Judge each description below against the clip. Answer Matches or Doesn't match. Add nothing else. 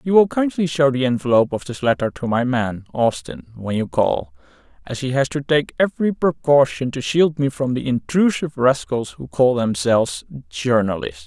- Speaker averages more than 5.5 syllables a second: Doesn't match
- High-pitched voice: Doesn't match